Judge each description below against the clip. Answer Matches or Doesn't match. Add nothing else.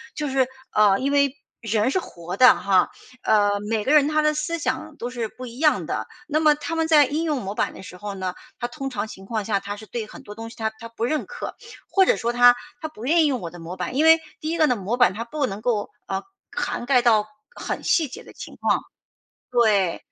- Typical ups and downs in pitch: Doesn't match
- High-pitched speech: Matches